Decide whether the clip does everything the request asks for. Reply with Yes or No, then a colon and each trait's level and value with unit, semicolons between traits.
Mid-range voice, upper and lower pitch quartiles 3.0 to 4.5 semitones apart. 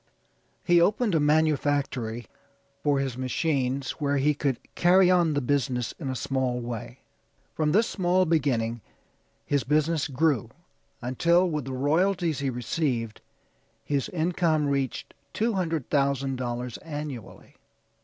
Yes: medium, 145 Hz; average, 4.2 semitones